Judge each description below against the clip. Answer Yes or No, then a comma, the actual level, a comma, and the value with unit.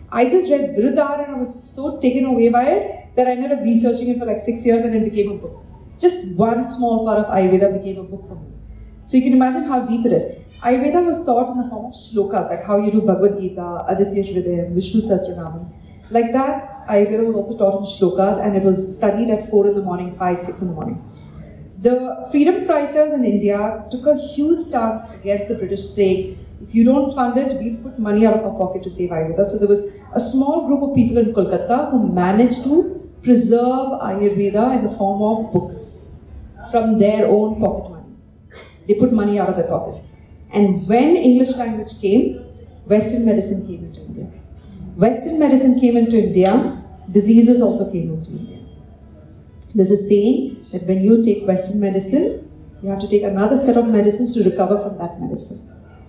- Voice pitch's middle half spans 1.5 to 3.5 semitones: No, average, 4.1 semitones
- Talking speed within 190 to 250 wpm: Yes, average, 200 wpm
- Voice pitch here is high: Yes, high, 215 Hz